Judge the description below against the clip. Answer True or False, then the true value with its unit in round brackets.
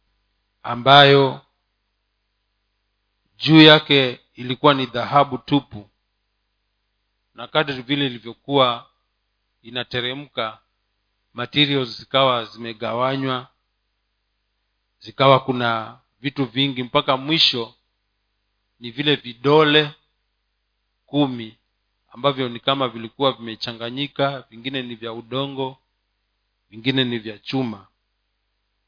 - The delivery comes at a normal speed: False (80 wpm)